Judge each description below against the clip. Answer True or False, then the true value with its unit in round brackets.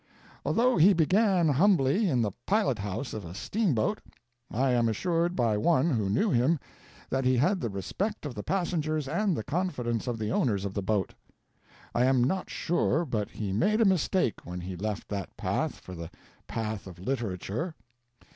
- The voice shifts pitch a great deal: True (8.7 semitones)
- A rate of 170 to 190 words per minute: True (175 wpm)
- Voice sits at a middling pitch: False (130 Hz)